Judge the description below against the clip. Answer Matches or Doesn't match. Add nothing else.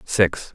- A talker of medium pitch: Doesn't match